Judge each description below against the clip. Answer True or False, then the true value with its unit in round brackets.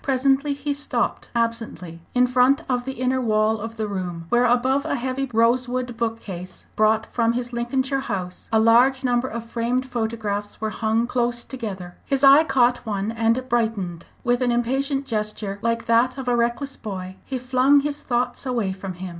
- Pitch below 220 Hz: False (240 Hz)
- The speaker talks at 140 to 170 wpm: False (180 wpm)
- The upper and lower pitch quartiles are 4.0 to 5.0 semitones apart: False (2.8 semitones)